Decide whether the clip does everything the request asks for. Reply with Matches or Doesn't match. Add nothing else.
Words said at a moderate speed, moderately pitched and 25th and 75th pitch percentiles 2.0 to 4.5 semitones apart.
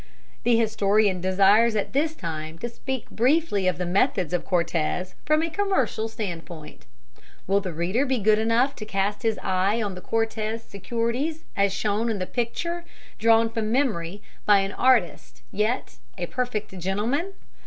Doesn't match